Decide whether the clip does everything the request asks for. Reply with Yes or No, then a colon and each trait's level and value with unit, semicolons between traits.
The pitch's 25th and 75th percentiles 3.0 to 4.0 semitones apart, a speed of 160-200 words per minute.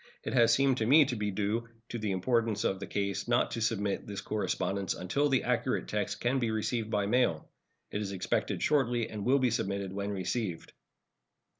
Yes: average, 3.4 semitones; average, 195 wpm